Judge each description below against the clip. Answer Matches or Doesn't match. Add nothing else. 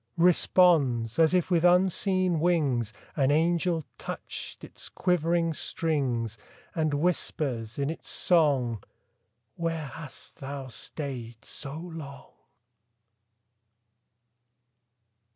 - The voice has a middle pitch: Matches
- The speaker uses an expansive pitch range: Doesn't match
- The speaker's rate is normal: Doesn't match